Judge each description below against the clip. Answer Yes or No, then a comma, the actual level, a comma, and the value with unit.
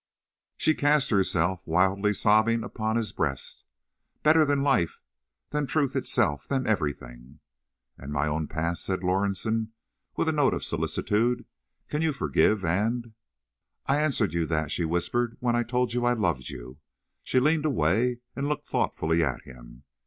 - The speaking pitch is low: Yes, low, 105 Hz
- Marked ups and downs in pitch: Yes, wide, 7.3 semitones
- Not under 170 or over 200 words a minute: No, average, 145 wpm